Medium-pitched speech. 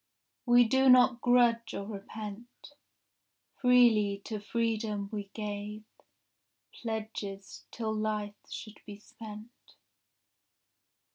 No: high, 220 Hz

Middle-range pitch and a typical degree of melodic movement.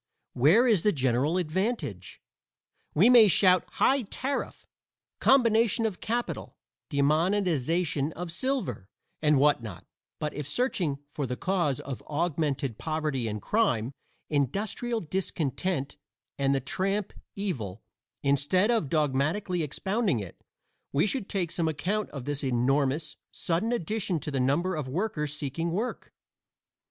No: medium, 160 Hz; wide, 6.3 semitones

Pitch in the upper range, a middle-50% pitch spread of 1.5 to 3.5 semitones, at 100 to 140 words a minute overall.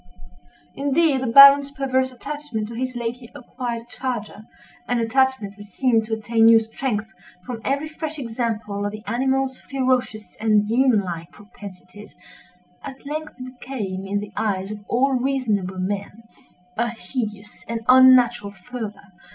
No: high, 235 Hz; average, 3.9 semitones; slow, 135 wpm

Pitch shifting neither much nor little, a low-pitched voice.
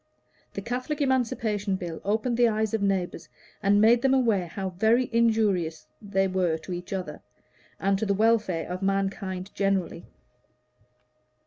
No: average, 3.2 semitones; high, 200 Hz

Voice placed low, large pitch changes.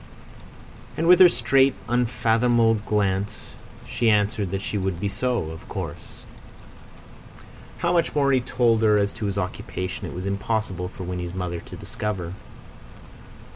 No: low, 105 Hz; average, 4.3 semitones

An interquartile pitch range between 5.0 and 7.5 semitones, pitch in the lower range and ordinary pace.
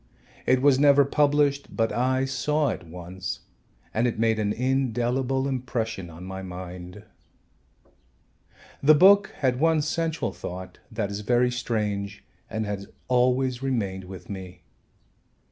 No: wide, 5.4 semitones; low, 120 Hz; slow, 130 wpm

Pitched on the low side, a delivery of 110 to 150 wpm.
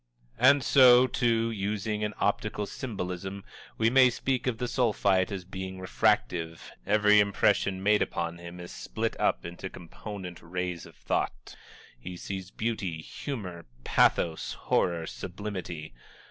Yes: low, 100 Hz; slow, 135 wpm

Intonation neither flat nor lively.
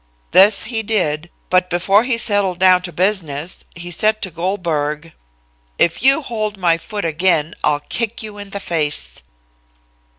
Yes: average, 3.9 semitones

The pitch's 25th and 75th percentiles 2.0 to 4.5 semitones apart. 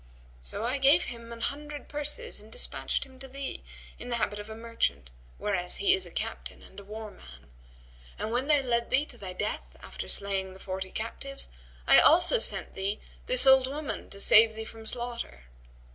No: average, 5.0 semitones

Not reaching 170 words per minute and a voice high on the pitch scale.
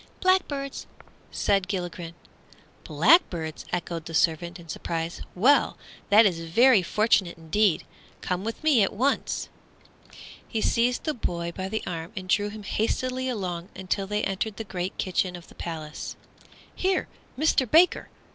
Yes: average, 145 wpm; high, 195 Hz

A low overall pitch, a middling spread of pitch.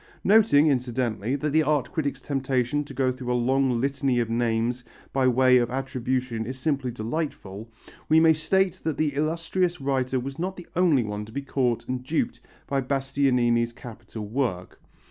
Yes: low, 130 Hz; average, 3.2 semitones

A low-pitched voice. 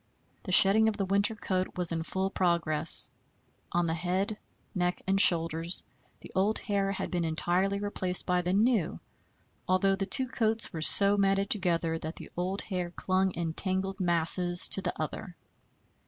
No: medium, 185 Hz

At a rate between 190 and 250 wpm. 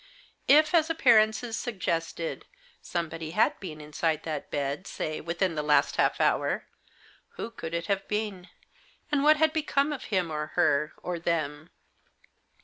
No: average, 145 wpm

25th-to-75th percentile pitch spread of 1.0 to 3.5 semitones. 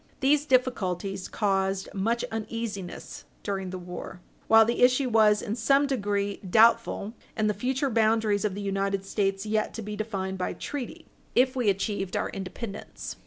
Yes: average, 3.0 semitones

